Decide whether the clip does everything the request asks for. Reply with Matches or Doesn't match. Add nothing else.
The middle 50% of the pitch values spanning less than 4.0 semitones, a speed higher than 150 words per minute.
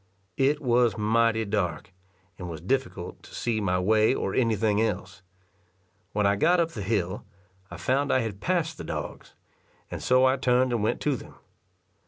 Doesn't match